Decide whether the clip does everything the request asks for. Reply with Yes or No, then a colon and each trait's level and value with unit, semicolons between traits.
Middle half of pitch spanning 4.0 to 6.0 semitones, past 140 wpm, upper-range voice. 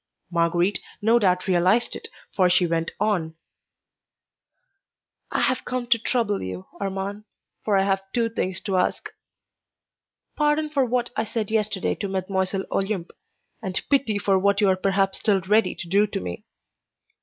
No: average, 2.8 semitones; average, 155 wpm; high, 195 Hz